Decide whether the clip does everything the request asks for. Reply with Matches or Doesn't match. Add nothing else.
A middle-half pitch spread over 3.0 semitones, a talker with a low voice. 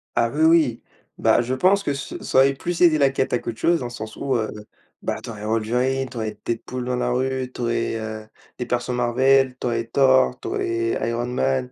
Doesn't match